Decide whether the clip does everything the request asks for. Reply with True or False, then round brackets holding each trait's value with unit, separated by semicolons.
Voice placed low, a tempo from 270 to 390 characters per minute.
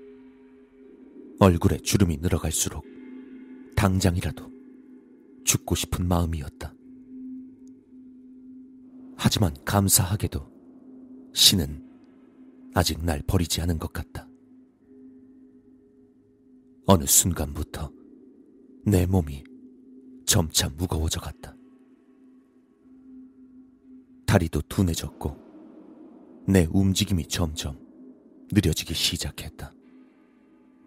False (130 Hz; 165 characters per minute)